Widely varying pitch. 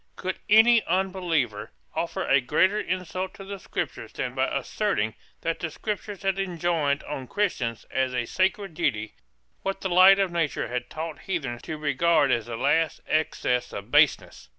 Yes: wide, 6.4 semitones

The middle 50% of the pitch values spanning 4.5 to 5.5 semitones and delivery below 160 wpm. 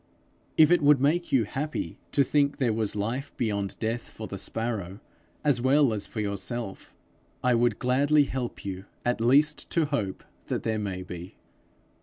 No: average, 5.2 semitones; average, 170 wpm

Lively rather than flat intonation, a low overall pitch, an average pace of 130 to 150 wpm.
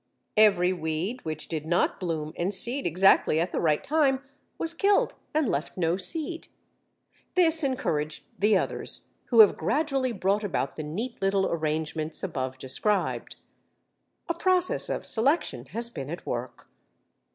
No: wide, 8.8 semitones; high, 190 Hz; average, 145 wpm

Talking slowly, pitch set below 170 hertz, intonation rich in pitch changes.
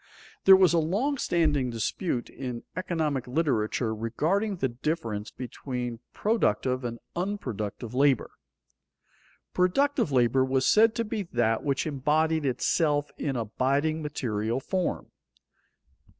Yes: slow, 115 wpm; medium, 140 Hz; wide, 6.0 semitones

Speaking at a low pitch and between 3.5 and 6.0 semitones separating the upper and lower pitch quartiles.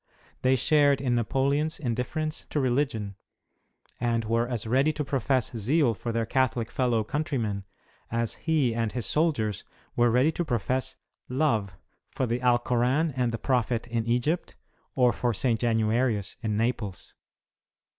No: low, 120 Hz; average, 3.0 semitones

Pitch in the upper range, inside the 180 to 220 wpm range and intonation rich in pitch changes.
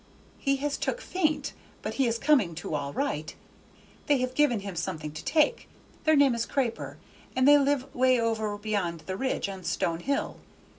Yes: high, 235 Hz; average, 185 wpm; wide, 7.0 semitones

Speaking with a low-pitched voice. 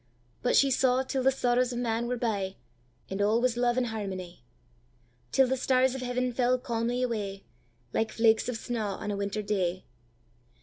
No: high, 225 Hz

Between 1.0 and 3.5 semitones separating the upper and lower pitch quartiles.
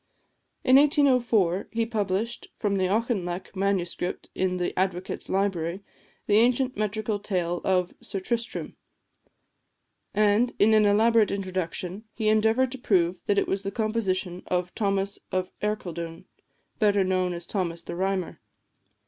Yes: average, 3.0 semitones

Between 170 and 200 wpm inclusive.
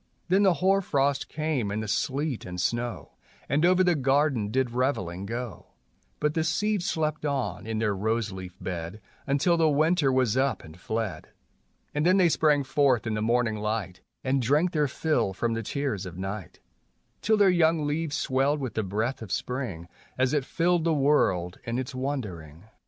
Yes: average, 185 wpm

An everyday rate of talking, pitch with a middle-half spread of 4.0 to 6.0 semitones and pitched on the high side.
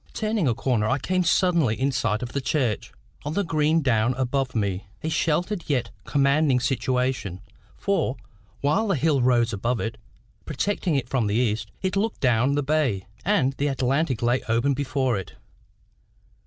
No: average, 170 wpm; average, 4.5 semitones; low, 135 Hz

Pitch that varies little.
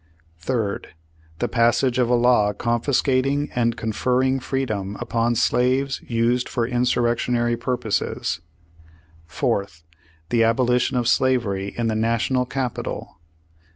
Yes: narrow, 1.9 semitones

